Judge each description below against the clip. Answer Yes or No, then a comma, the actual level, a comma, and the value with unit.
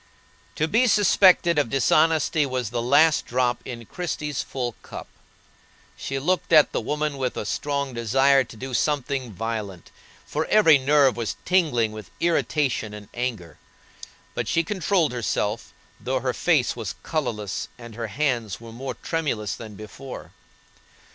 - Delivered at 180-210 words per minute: No, average, 150 wpm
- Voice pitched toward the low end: Yes, low, 130 Hz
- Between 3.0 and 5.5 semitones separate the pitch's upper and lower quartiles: Yes, average, 4.8 semitones